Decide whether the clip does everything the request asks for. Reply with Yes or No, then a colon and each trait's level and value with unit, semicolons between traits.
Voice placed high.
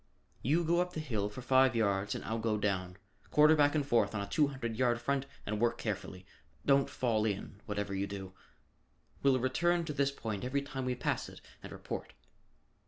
No: low, 120 Hz